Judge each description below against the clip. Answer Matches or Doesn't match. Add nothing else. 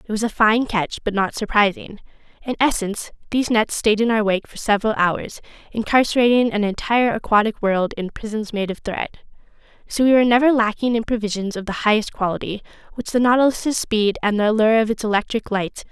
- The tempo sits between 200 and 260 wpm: Matches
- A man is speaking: Doesn't match